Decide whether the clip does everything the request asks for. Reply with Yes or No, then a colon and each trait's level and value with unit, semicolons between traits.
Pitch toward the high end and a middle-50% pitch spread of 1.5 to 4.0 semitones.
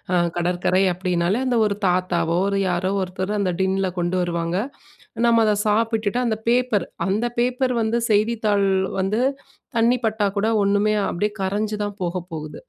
Yes: high, 200 Hz; average, 3.2 semitones